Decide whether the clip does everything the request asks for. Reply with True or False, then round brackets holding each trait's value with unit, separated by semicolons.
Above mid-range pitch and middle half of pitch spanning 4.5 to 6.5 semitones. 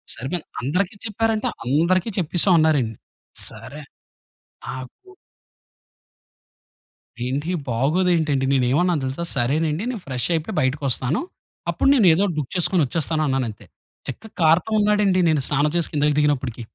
False (150 Hz; 5.3 semitones)